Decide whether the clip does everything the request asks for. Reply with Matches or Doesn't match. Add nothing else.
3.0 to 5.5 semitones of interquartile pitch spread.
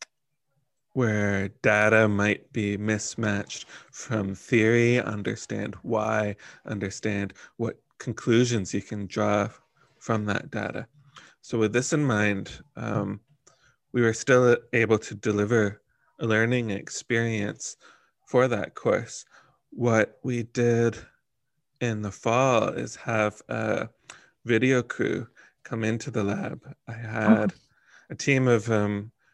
Doesn't match